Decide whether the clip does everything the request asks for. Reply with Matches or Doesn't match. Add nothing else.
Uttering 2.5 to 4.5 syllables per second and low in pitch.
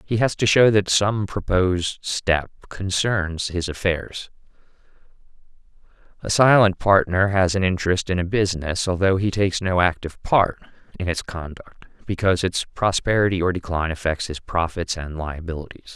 Doesn't match